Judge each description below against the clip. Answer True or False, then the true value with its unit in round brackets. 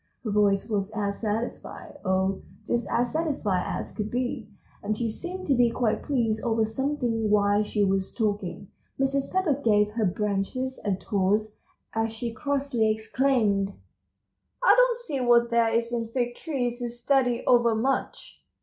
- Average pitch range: True (3.5 semitones)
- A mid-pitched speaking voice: False (230 Hz)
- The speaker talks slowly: False (160 wpm)